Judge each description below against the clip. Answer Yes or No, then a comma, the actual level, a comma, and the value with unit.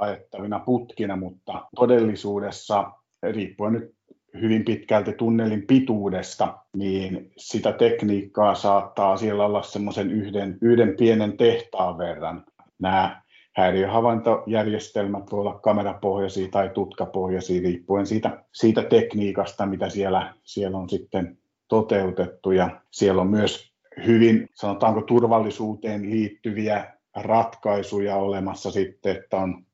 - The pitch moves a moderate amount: No, narrow, 2.2 semitones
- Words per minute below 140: Yes, average, 105 wpm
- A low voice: Yes, low, 100 Hz